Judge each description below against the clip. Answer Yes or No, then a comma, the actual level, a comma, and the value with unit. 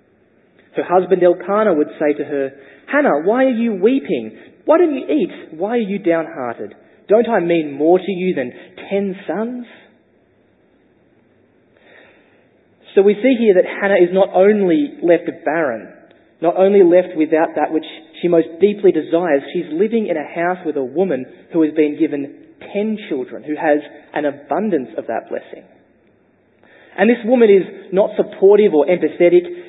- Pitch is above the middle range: No, medium, 180 Hz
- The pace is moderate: Yes, average, 160 wpm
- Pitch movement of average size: Yes, average, 4.8 semitones